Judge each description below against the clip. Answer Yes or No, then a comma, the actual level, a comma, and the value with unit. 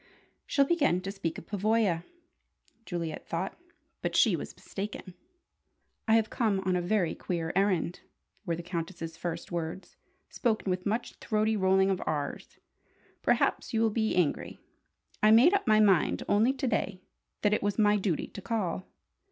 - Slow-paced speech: No, average, 160 wpm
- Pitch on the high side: Yes, high, 195 Hz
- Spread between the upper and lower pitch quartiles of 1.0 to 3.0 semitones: No, average, 3.8 semitones